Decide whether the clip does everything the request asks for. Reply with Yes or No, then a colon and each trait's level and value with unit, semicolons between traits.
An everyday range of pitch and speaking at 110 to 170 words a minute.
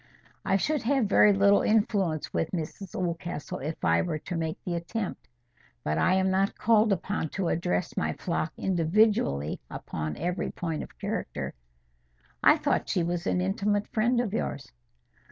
Yes: average, 3.7 semitones; average, 160 wpm